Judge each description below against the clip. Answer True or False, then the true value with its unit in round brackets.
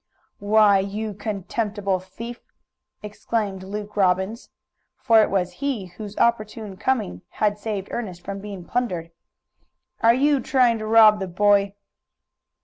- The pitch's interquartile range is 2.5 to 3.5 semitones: True (2.8 semitones)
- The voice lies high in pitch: True (210 Hz)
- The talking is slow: True (130 wpm)